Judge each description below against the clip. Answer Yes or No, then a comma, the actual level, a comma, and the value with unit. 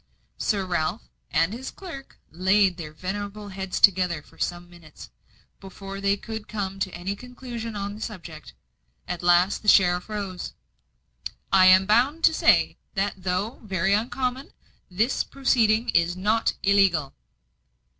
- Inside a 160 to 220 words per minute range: No, average, 140 wpm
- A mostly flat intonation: No, average, 3.3 semitones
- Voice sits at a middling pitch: No, high, 195 Hz